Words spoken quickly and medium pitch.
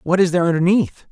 Yes: fast, 215 wpm; medium, 175 Hz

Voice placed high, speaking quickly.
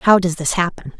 No: medium, 175 Hz; fast, 240 wpm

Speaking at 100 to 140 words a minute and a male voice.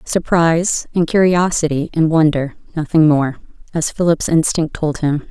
No: slow, 135 wpm; female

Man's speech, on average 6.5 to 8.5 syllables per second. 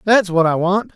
No: male; 4.9 syllables/s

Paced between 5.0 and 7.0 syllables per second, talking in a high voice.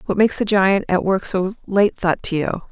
Yes: 5.1 syllables/s; high, 195 Hz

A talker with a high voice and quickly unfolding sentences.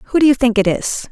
Yes: high, 245 Hz; fast, 325 wpm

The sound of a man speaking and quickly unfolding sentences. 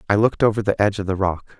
Yes: male; fast, 300 wpm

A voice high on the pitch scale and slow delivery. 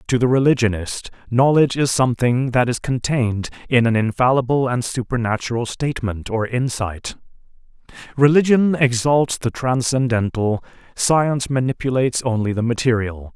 No: low, 125 Hz; slow, 115 wpm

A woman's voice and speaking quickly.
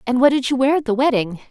Yes: female; fast, 320 wpm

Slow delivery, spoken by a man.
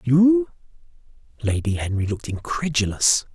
Yes: slow, 90 wpm; male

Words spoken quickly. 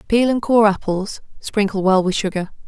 No: average, 180 wpm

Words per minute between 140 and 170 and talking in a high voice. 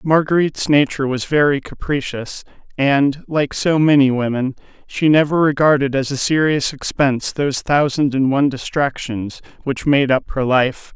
No: average, 150 wpm; medium, 140 Hz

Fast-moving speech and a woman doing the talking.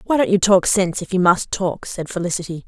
Yes: fast, 245 wpm; female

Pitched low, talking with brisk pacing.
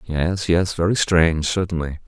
No: very low, 85 Hz; average, 145 wpm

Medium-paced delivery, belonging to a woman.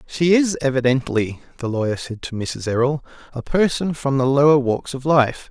No: average, 185 wpm; male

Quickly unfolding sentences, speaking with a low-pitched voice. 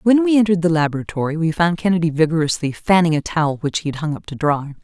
No: fast, 235 wpm; medium, 165 Hz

